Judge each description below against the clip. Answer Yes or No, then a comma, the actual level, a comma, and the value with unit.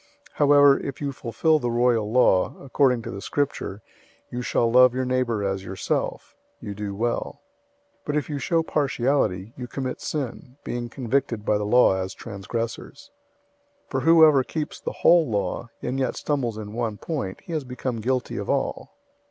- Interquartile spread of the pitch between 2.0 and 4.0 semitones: No, average, 4.4 semitones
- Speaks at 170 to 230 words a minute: Yes, average, 180 wpm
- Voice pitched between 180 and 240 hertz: No, low, 125 Hz